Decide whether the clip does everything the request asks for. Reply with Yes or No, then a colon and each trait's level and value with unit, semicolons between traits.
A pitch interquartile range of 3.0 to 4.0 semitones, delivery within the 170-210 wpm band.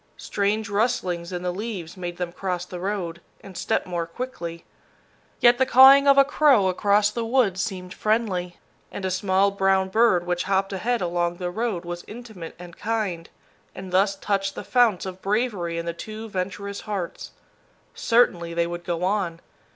Yes: average, 3.4 semitones; average, 175 wpm